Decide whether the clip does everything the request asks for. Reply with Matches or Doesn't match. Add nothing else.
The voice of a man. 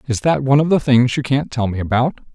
Matches